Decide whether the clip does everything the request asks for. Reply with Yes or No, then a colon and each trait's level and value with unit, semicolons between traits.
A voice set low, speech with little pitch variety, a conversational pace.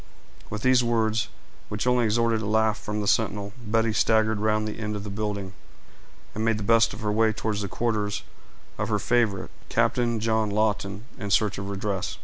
Yes: low, 110 Hz; narrow, 1.4 semitones; average, 190 wpm